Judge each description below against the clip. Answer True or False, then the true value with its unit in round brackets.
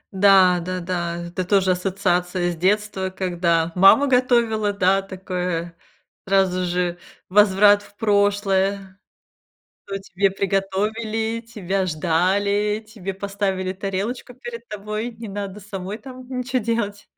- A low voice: False (195 Hz)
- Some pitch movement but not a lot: False (2.3 semitones)